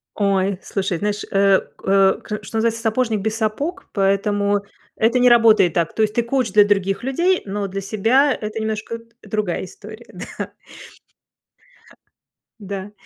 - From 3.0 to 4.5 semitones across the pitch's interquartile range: No, narrow, 2.5 semitones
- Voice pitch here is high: Yes, high, 210 Hz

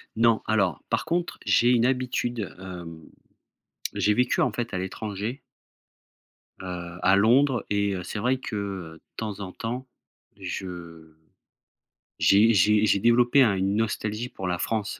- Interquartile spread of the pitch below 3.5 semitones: No, average, 4.1 semitones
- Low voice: Yes, low, 105 Hz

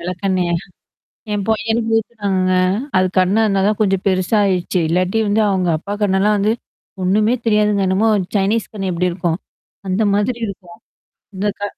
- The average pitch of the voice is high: Yes, high, 195 Hz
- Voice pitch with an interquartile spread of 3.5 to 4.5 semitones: No, narrow, 2.4 semitones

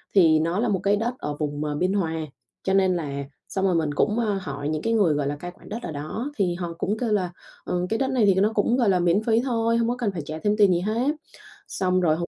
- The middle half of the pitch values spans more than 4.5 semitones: Yes, average, 5.0 semitones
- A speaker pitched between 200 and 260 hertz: No, high, 190 Hz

